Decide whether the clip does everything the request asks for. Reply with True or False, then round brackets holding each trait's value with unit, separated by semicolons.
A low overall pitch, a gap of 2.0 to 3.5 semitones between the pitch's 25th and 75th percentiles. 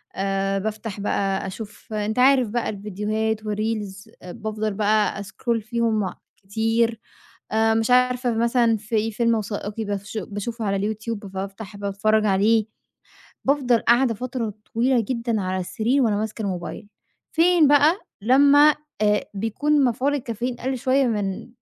False (220 Hz; 2.7 semitones)